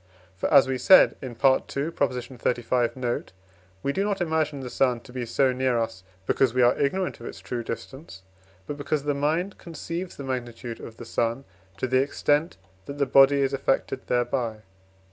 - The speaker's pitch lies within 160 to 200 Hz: No, low, 130 Hz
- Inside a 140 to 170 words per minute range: No, average, 185 wpm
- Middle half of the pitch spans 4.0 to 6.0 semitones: No, average, 3.0 semitones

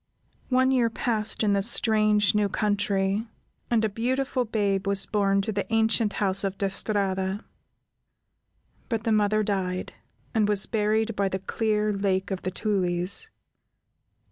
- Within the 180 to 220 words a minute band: No, average, 145 wpm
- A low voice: No, high, 210 Hz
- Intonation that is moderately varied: No, narrow, 2.1 semitones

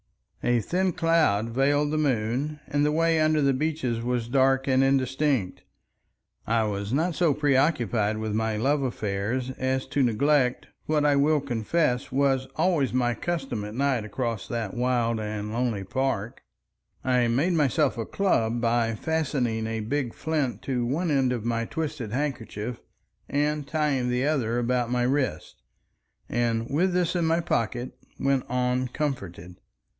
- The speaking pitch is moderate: No, low, 130 Hz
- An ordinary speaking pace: Yes, average, 155 wpm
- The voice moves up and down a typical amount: Yes, average, 4.1 semitones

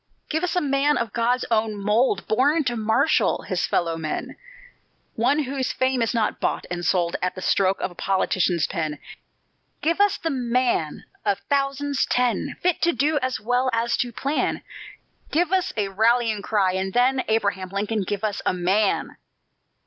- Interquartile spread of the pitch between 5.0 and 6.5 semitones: Yes, wide, 5.6 semitones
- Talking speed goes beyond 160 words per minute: Yes, average, 170 wpm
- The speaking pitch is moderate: No, high, 230 Hz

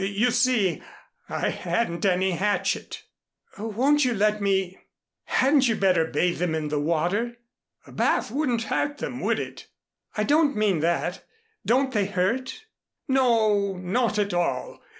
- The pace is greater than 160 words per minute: No, average, 145 wpm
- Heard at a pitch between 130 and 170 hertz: No, high, 210 Hz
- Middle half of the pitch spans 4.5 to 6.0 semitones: Yes, average, 5.2 semitones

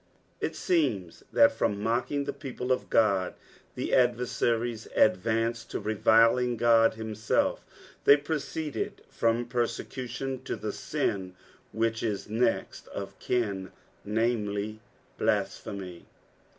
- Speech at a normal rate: No, slow, 110 wpm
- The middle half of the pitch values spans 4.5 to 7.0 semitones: No, average, 2.8 semitones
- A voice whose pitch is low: Yes, low, 115 Hz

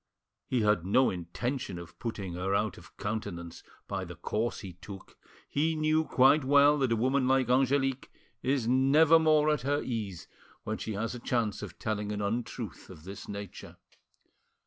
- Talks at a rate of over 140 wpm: Yes, average, 175 wpm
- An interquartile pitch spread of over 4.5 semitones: Yes, average, 5.1 semitones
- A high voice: No, low, 120 Hz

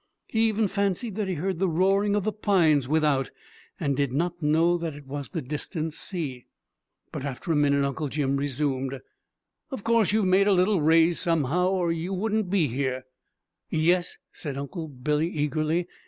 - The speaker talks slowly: No, average, 175 wpm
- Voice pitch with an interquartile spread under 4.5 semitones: No, average, 4.8 semitones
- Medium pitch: Yes, medium, 165 Hz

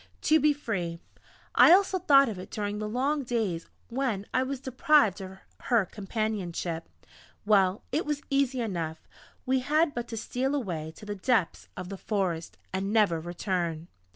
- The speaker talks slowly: No, average, 165 wpm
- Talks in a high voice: Yes, high, 215 Hz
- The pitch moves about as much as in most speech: No, wide, 6.3 semitones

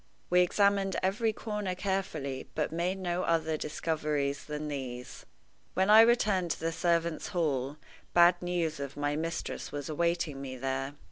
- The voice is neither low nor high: Yes, medium, 165 Hz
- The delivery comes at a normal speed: Yes, average, 150 wpm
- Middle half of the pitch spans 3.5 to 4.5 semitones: Yes, average, 4.0 semitones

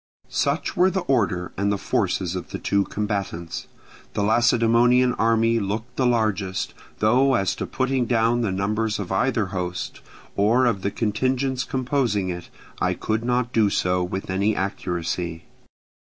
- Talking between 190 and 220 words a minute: No, average, 155 wpm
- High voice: No, low, 110 Hz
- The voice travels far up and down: No, average, 4.1 semitones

